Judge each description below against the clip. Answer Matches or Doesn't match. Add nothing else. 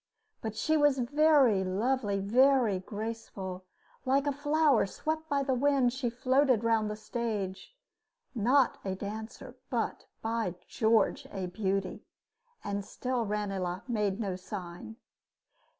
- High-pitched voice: Matches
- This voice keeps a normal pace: Doesn't match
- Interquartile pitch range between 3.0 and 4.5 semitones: Doesn't match